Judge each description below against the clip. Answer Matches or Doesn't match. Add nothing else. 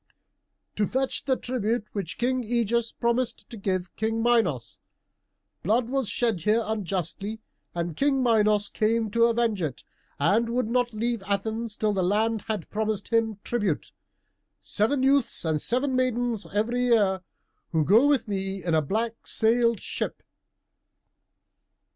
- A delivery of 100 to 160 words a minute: Matches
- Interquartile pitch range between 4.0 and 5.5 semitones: Doesn't match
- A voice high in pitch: Matches